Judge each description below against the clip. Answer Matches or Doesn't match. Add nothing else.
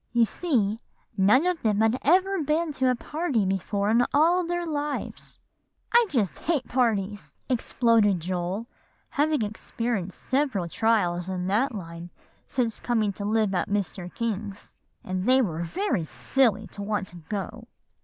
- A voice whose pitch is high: Matches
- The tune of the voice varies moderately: Doesn't match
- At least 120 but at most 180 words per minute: Matches